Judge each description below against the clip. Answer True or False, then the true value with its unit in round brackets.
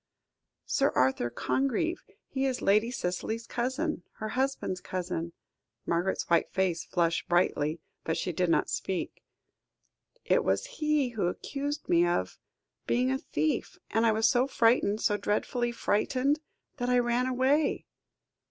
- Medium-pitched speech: False (220 Hz)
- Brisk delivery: False (140 wpm)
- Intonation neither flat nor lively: False (6.8 semitones)